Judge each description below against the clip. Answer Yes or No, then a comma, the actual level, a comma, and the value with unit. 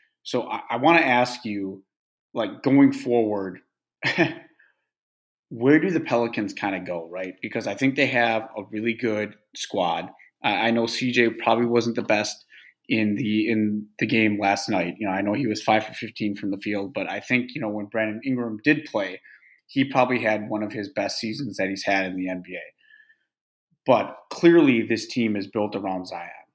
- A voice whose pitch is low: Yes, low, 110 Hz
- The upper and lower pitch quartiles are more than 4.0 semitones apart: No, average, 2.8 semitones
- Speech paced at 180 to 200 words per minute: Yes, average, 195 wpm